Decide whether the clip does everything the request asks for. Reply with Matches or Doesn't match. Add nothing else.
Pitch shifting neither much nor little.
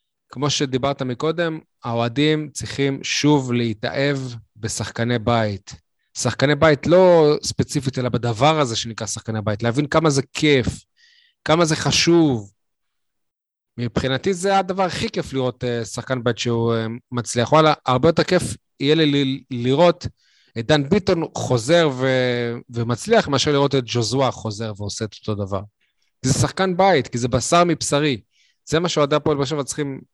Matches